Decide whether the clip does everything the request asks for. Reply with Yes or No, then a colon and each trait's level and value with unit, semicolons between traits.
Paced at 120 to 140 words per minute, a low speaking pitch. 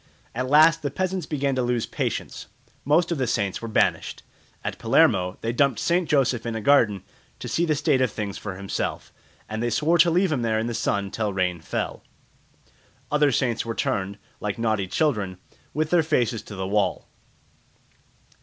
No: average, 185 wpm; low, 120 Hz